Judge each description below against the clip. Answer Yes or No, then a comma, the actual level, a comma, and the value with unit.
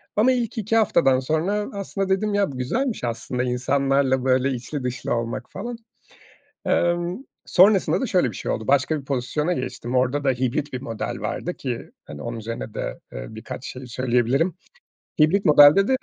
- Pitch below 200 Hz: Yes, medium, 140 Hz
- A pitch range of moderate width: No, wide, 7.1 semitones